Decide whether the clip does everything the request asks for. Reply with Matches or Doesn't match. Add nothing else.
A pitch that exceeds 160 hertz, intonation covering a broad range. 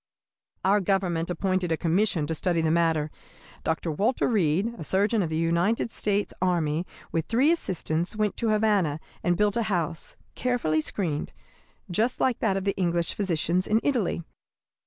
Doesn't match